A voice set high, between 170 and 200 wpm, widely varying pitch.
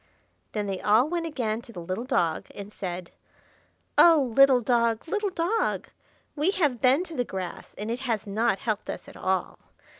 Yes: high, 235 Hz; average, 180 wpm; wide, 6.3 semitones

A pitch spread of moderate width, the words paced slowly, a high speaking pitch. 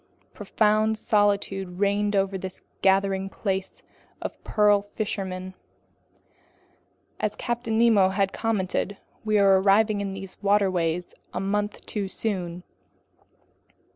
No: narrow, 1.6 semitones; slow, 110 wpm; high, 200 Hz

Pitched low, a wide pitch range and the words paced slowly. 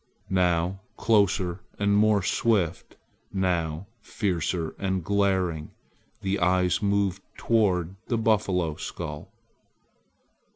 No: very low, 95 Hz; narrow, 2.5 semitones; slow, 90 wpm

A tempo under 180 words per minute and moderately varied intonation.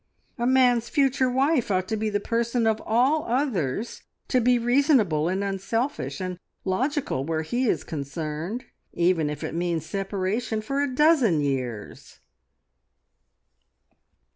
No: slow, 135 wpm; wide, 6.8 semitones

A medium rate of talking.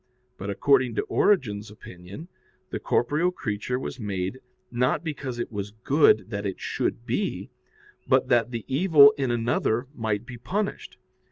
Yes: average, 150 wpm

